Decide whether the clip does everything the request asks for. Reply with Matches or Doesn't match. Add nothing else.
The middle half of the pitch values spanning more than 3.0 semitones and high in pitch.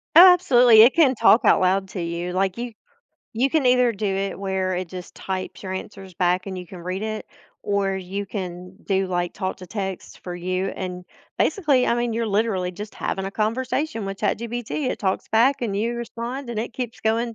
Matches